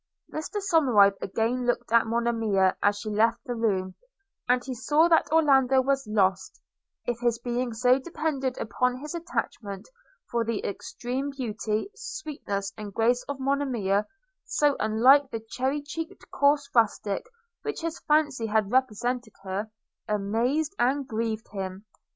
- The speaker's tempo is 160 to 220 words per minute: No, average, 140 wpm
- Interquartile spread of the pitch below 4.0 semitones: No, average, 4.4 semitones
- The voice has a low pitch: No, high, 240 Hz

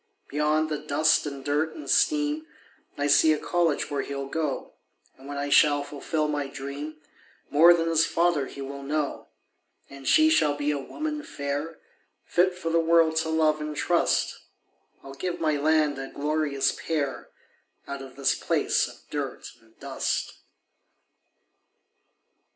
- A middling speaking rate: Yes, average, 155 wpm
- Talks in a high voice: No, medium, 150 Hz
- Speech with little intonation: Yes, narrow, 2.3 semitones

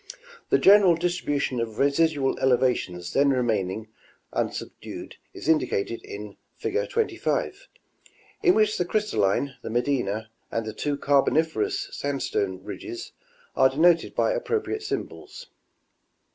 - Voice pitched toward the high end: No, medium, 140 Hz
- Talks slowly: Yes, slow, 115 wpm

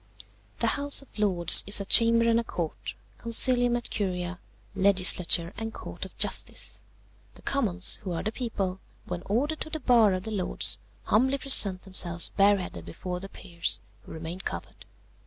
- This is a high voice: Yes, high, 200 Hz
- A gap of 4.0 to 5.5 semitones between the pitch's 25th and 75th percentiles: Yes, average, 4.3 semitones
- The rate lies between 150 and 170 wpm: Yes, average, 165 wpm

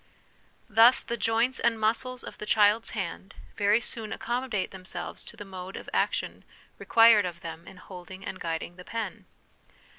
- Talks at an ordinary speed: Yes, average, 160 wpm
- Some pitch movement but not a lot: Yes, average, 3.6 semitones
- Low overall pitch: No, high, 210 Hz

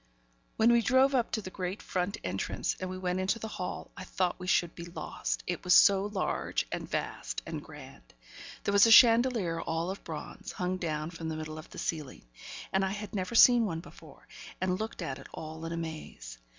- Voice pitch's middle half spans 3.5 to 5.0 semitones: Yes, average, 3.9 semitones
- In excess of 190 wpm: Yes, fast, 205 wpm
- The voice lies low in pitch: No, medium, 185 Hz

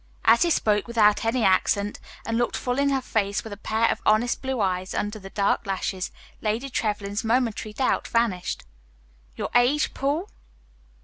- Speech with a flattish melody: No, average, 3.3 semitones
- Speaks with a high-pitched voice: Yes, high, 220 Hz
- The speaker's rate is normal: Yes, average, 170 wpm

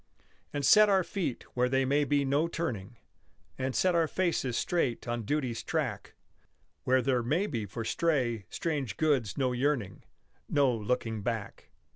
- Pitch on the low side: Yes, low, 130 Hz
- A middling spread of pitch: Yes, average, 4.4 semitones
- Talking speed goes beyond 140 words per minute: Yes, average, 155 wpm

